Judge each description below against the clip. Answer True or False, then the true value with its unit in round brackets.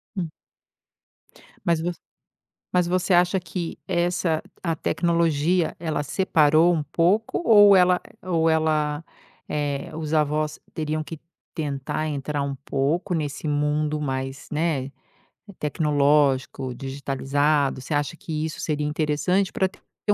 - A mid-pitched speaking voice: True (155 Hz)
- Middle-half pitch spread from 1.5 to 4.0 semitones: True (2.8 semitones)